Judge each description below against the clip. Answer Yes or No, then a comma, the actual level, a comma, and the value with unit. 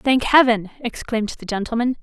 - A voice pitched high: Yes, high, 235 Hz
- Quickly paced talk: No, average, 150 wpm